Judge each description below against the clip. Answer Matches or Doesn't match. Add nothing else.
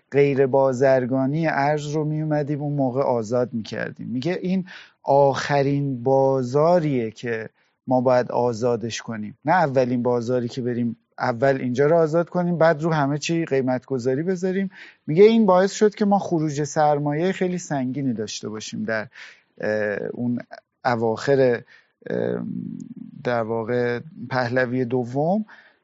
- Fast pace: Doesn't match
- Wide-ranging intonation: Doesn't match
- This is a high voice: Doesn't match